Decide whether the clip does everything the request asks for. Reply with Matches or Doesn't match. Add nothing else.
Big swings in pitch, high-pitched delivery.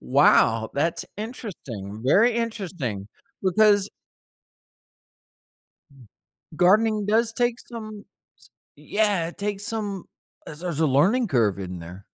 Matches